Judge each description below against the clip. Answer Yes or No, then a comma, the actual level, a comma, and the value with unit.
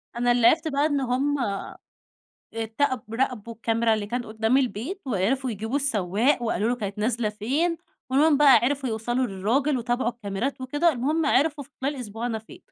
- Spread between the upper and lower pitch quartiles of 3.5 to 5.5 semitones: Yes, average, 4.1 semitones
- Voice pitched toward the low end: No, high, 245 Hz